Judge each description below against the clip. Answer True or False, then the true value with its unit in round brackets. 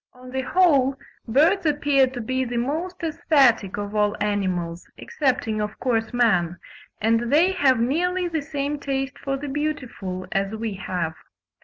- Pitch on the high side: True (255 Hz)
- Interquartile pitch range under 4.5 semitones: False (5.5 semitones)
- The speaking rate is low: False (155 wpm)